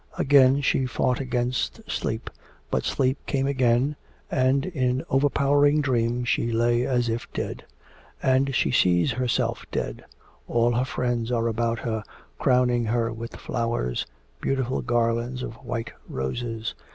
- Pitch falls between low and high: No, low, 125 Hz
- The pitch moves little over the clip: Yes, narrow, 2.1 semitones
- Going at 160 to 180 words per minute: No, slow, 135 wpm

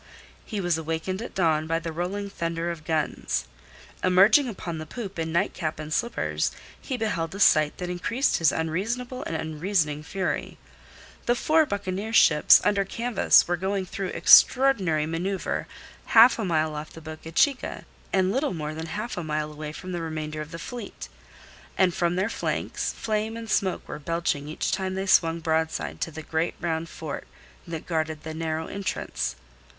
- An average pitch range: Yes, average, 4.0 semitones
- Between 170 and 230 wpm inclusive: Yes, average, 175 wpm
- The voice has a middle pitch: Yes, medium, 170 Hz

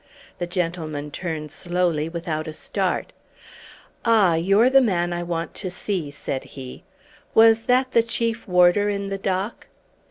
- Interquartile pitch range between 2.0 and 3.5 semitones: No, average, 4.3 semitones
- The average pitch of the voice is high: No, medium, 180 Hz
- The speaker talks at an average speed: Yes, average, 150 wpm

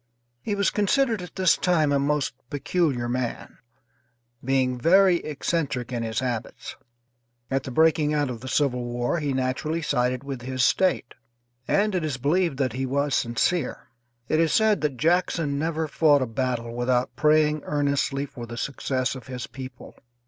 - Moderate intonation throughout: Yes, average, 4.1 semitones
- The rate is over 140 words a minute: Yes, average, 165 wpm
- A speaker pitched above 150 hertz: No, medium, 140 Hz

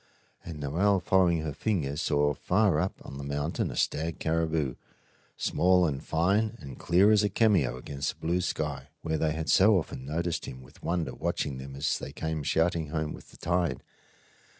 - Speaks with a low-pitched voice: Yes, very low, 80 Hz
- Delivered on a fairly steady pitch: No, average, 3.8 semitones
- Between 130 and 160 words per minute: No, average, 185 wpm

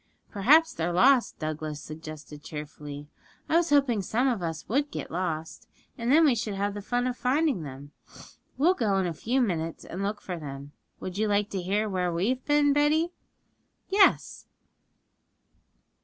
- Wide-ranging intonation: Yes, wide, 8.3 semitones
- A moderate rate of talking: Yes, average, 170 wpm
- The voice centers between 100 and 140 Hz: No, high, 205 Hz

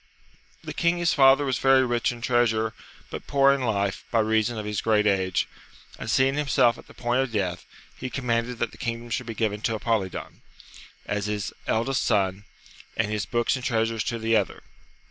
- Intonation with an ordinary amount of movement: Yes, average, 3.0 semitones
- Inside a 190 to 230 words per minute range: Yes, average, 200 wpm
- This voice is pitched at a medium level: No, low, 115 Hz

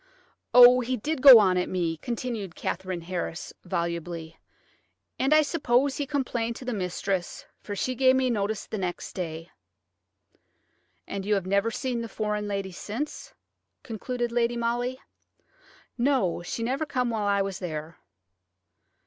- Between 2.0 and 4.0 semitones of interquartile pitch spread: No, average, 5.2 semitones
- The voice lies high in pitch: Yes, high, 220 Hz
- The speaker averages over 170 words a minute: No, average, 150 wpm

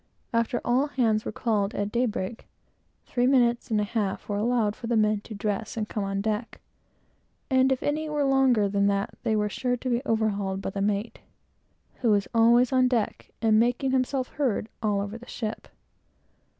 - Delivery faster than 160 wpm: Yes, average, 190 wpm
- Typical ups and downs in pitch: Yes, average, 3.1 semitones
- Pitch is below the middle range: No, high, 225 Hz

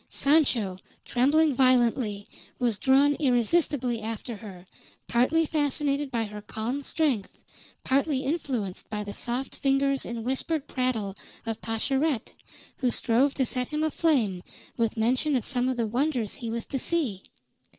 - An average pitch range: Yes, average, 3.9 semitones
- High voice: Yes, very high, 255 Hz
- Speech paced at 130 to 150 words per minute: Yes, average, 140 wpm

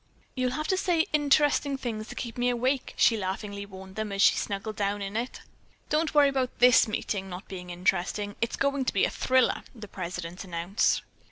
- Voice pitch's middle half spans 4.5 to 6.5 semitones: Yes, average, 5.0 semitones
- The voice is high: Yes, high, 215 Hz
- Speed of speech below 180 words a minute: No, average, 195 wpm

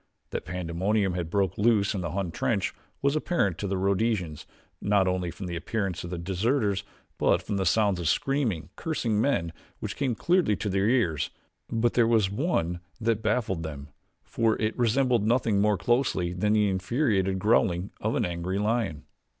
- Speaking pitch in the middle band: No, low, 100 Hz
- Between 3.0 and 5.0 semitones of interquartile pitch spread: Yes, average, 4.2 semitones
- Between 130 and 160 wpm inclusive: No, average, 175 wpm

